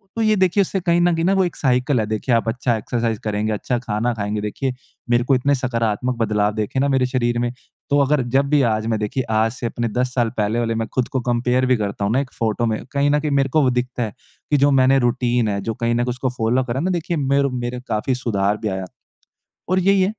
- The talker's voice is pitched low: Yes, low, 125 Hz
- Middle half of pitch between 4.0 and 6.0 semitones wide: No, average, 3.6 semitones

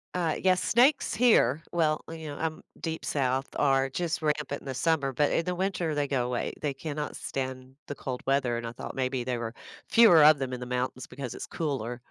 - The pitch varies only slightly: No, average, 4.0 semitones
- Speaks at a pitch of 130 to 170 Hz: Yes, medium, 140 Hz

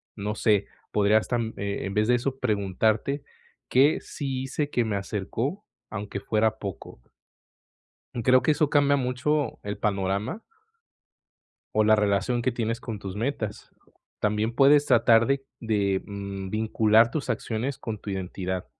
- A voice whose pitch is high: No, low, 110 Hz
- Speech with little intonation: No, average, 4.1 semitones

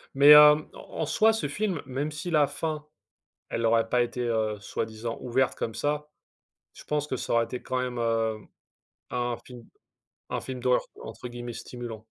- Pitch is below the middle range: Yes, low, 125 Hz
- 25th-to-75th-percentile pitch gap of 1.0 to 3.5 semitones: No, average, 4.3 semitones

